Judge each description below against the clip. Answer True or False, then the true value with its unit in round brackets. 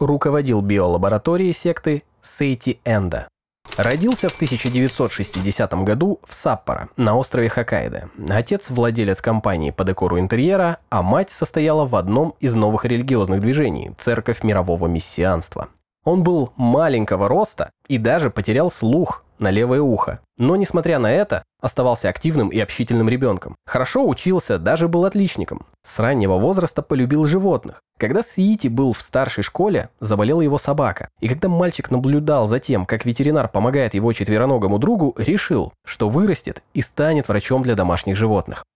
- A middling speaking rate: True (140 wpm)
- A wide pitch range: True (6.3 semitones)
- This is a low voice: True (125 Hz)